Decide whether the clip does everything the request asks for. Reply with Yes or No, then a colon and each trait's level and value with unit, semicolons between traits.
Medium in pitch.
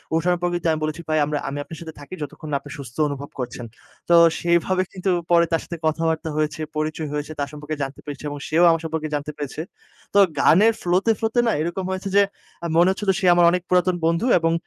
Yes: medium, 160 Hz